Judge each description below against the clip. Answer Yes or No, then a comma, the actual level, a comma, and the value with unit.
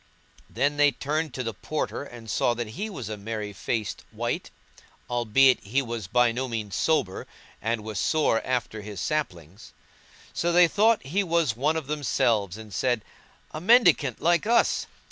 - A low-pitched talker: Yes, low, 125 Hz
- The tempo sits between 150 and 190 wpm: Yes, average, 170 wpm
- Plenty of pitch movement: Yes, wide, 5.9 semitones